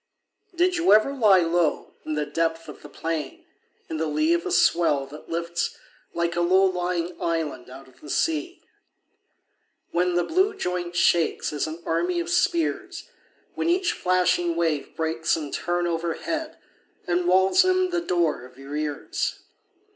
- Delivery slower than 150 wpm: No, average, 165 wpm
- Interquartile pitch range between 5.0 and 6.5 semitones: Yes, average, 5.3 semitones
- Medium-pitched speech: Yes, medium, 175 Hz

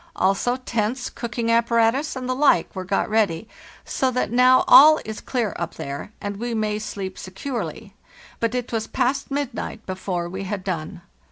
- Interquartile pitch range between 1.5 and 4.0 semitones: No, average, 4.5 semitones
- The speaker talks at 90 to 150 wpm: No, average, 175 wpm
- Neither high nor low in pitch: No, high, 225 Hz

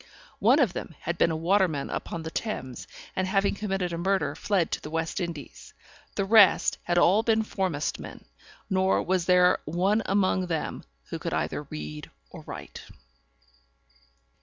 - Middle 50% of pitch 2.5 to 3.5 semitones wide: Yes, average, 3.2 semitones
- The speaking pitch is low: No, medium, 185 Hz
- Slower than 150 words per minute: No, average, 160 wpm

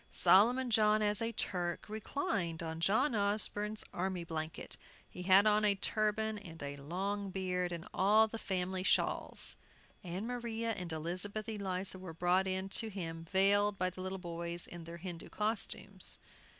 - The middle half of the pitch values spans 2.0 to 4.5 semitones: Yes, average, 3.3 semitones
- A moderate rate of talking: Yes, average, 160 wpm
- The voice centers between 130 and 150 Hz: No, high, 190 Hz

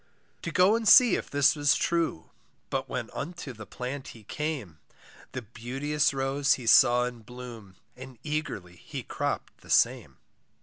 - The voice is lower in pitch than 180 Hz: Yes, low, 135 Hz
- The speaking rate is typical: Yes, average, 160 wpm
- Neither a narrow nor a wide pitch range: Yes, average, 4.1 semitones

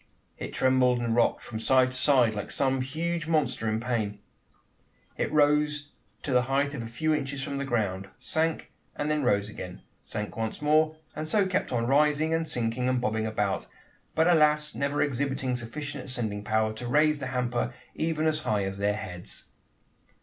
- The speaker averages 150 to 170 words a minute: No, average, 180 wpm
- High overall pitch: No, low, 130 Hz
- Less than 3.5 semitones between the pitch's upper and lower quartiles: No, average, 4.9 semitones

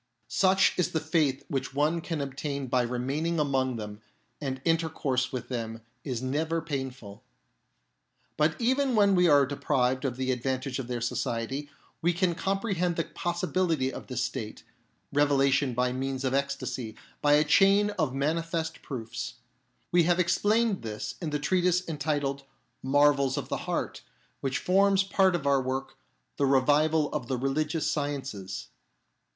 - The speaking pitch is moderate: Yes, medium, 145 Hz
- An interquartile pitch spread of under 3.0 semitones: No, average, 4.1 semitones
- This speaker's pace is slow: No, average, 155 wpm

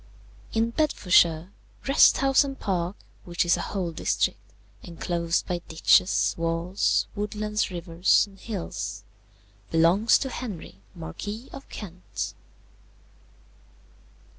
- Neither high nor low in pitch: Yes, medium, 180 Hz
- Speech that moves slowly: Yes, slow, 105 wpm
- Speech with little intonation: No, average, 4.1 semitones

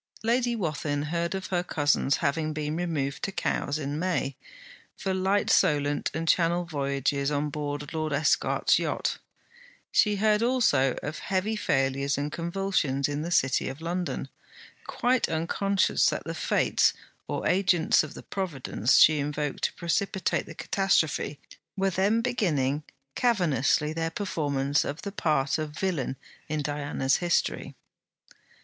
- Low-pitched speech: No, medium, 155 Hz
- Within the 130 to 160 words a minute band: Yes, average, 140 wpm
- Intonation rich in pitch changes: No, average, 4.7 semitones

